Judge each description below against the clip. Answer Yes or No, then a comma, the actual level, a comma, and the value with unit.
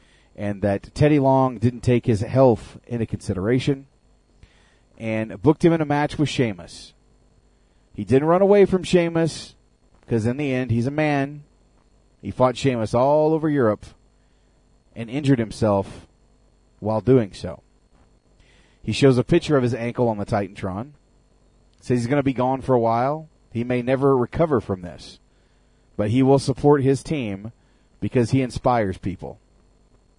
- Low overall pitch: Yes, low, 125 Hz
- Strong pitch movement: No, average, 5.0 semitones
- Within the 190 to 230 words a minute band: No, average, 155 wpm